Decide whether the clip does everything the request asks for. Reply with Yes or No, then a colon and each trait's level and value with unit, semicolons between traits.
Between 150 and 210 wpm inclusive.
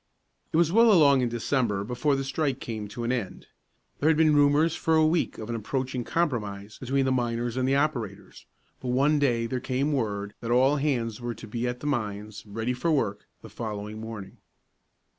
Yes: average, 200 wpm